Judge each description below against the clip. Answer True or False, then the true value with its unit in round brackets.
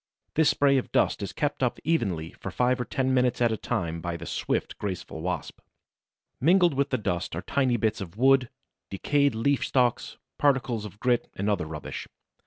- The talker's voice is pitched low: True (120 Hz)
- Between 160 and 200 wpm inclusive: True (190 wpm)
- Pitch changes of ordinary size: False (6.0 semitones)